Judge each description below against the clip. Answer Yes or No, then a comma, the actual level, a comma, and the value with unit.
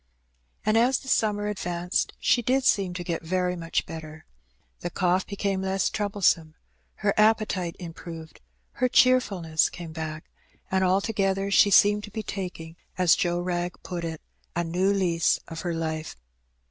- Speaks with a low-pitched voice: No, medium, 180 Hz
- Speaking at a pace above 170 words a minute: No, average, 160 wpm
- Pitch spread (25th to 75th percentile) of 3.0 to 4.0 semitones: Yes, average, 3.3 semitones